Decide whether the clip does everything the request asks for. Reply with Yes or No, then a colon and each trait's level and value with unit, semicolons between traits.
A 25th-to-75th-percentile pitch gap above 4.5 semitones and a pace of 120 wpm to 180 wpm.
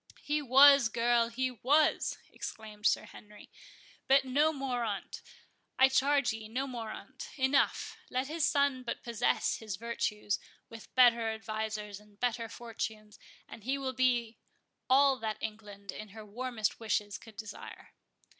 No: average, 3.3 semitones; average, 140 wpm